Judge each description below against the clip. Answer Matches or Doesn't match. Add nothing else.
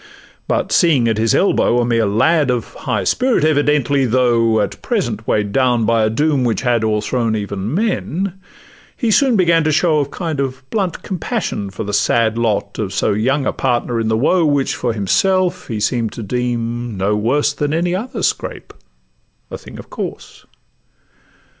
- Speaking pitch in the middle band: Doesn't match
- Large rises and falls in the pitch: Matches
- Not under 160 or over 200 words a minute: Matches